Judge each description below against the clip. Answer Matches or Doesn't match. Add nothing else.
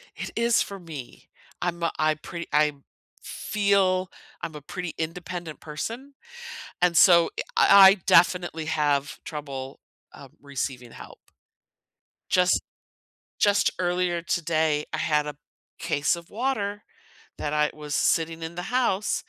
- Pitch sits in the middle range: Matches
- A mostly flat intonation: Doesn't match